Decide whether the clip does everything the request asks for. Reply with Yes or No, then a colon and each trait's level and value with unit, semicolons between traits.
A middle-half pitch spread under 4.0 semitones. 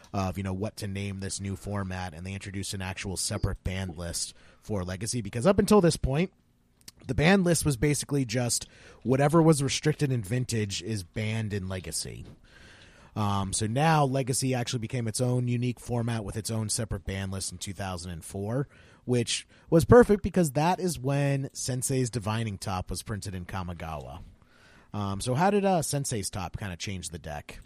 No: wide, 5.5 semitones